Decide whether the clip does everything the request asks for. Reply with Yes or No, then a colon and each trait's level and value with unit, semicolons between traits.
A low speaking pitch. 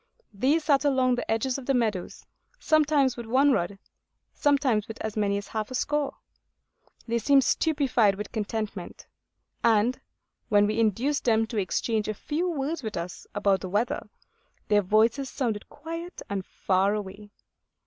No: high, 225 Hz